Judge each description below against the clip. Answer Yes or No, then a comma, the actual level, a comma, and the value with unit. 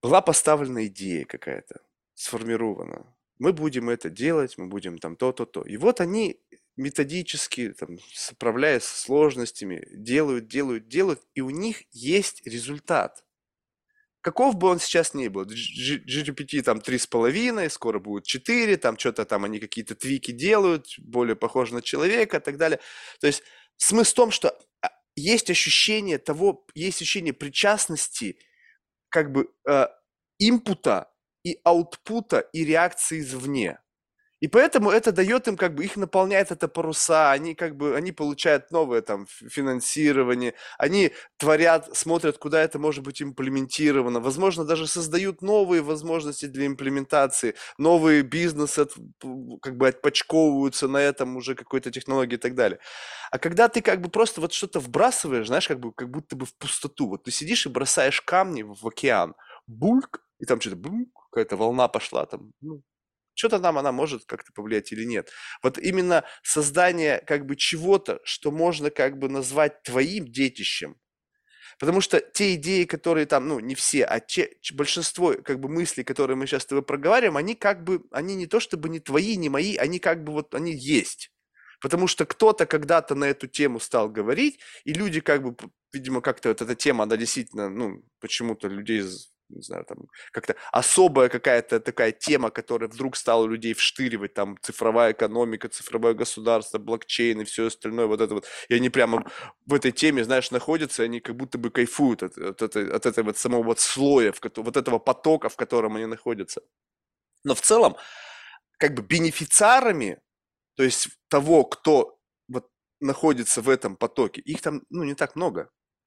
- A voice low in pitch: No, medium, 150 Hz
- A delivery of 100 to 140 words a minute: No, fast, 160 wpm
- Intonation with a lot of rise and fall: Yes, wide, 6.3 semitones